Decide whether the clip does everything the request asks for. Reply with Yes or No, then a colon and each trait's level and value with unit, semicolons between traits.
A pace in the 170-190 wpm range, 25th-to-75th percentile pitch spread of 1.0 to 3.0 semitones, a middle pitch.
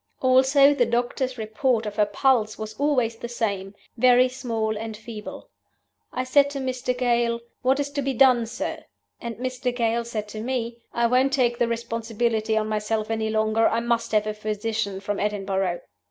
No: average, 180 wpm; average, 2.7 semitones; high, 230 Hz